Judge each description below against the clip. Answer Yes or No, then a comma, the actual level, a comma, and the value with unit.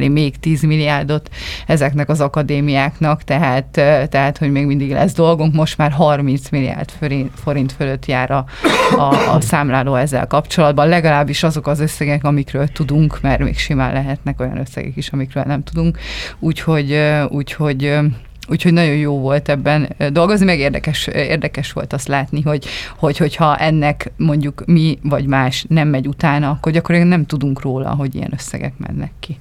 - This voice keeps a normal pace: No, fast, 160 wpm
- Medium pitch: Yes, medium, 145 Hz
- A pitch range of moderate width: No, narrow, 1.9 semitones